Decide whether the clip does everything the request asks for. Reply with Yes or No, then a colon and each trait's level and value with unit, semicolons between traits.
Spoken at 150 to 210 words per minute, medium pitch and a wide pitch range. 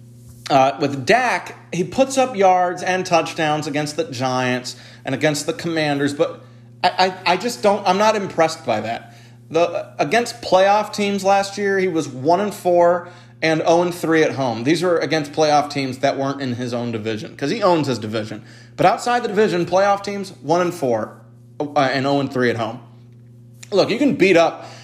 Yes: average, 195 wpm; medium, 155 Hz; wide, 6.6 semitones